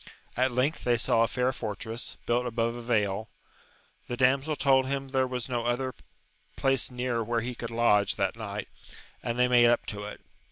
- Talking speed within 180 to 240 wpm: Yes, average, 190 wpm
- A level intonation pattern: Yes, narrow, 2.0 semitones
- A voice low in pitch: Yes, low, 120 Hz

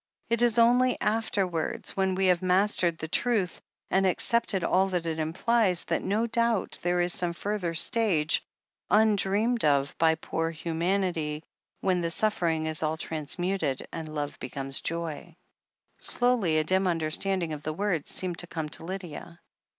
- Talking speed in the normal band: Yes, average, 160 wpm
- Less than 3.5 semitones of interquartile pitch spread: No, average, 3.8 semitones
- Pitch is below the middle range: No, medium, 180 Hz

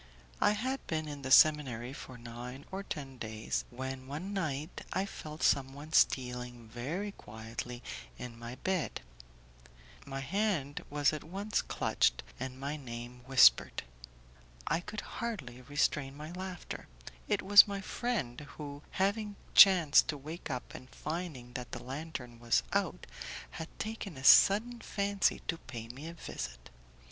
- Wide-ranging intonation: Yes, wide, 6.8 semitones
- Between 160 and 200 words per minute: No, average, 145 wpm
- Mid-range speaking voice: Yes, medium, 145 Hz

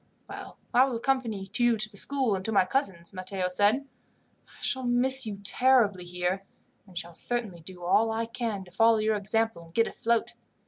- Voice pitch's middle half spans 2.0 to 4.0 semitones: No, average, 4.4 semitones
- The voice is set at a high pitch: Yes, high, 215 Hz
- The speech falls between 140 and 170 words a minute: No, average, 190 wpm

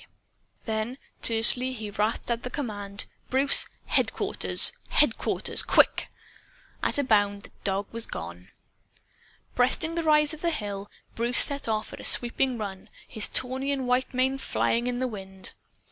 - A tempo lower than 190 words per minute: Yes, average, 150 wpm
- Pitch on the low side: No, high, 235 Hz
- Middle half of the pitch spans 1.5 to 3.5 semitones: No, average, 4.2 semitones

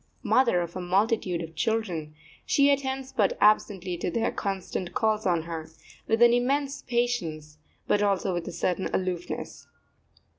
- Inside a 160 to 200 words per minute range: No, average, 150 wpm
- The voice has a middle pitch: No, high, 195 Hz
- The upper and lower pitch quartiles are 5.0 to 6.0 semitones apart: Yes, average, 5.3 semitones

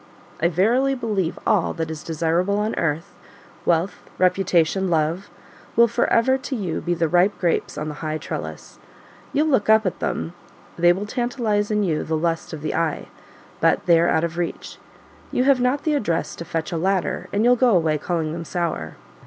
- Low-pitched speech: No, medium, 175 Hz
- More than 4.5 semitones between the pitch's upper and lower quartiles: Yes, average, 4.9 semitones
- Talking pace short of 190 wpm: No, average, 195 wpm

